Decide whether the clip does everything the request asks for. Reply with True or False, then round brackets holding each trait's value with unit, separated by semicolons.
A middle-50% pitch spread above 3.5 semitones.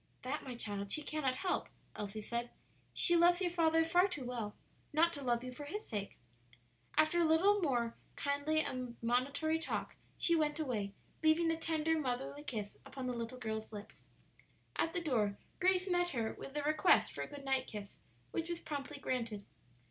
True (5.3 semitones)